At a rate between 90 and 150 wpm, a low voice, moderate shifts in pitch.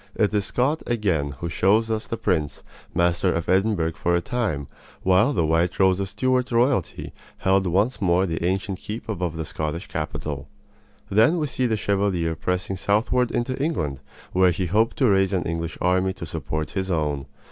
No: average, 180 wpm; very low, 95 Hz; average, 4.7 semitones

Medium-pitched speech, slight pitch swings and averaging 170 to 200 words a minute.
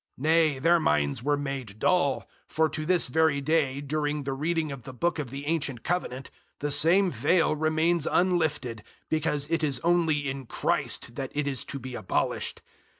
No: medium, 150 Hz; average, 3.1 semitones; average, 180 wpm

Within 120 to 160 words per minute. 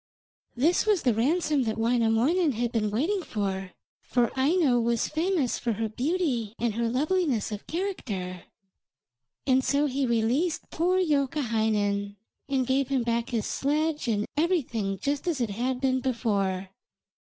Yes: average, 145 wpm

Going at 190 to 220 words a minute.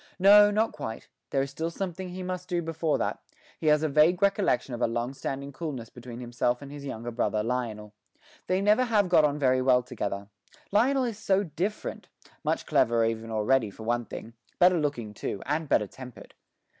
Yes: average, 195 wpm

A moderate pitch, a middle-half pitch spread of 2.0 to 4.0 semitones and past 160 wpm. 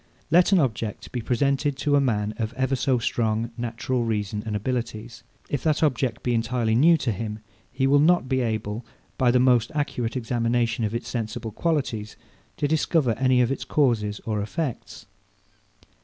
No: low, 120 Hz; average, 3.2 semitones; average, 170 wpm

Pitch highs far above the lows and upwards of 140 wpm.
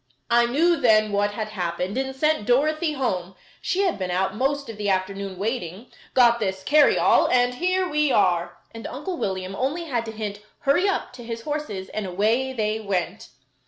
Yes: wide, 5.9 semitones; average, 185 wpm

